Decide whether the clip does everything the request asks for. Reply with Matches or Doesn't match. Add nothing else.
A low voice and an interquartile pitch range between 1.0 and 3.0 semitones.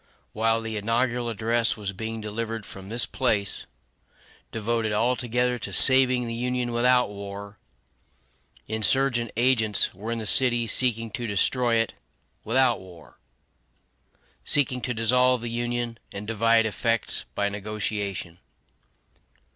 Matches